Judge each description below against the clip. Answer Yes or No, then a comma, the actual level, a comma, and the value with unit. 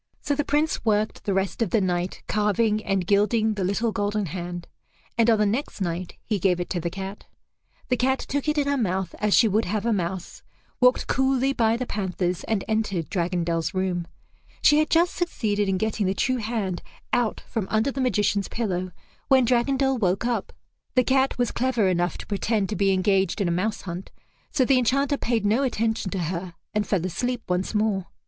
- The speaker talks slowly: No, average, 200 wpm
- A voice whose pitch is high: Yes, high, 210 Hz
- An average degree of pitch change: Yes, average, 4.5 semitones